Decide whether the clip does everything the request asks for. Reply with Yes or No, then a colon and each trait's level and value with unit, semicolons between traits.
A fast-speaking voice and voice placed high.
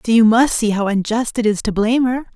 Yes: fast, 280 wpm; high, 225 Hz